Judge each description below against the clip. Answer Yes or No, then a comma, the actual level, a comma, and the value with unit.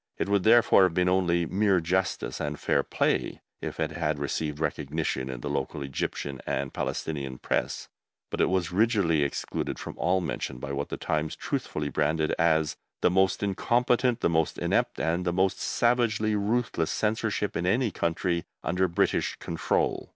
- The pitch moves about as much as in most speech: Yes, average, 4.5 semitones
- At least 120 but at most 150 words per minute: No, average, 165 wpm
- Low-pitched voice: Yes, very low, 85 Hz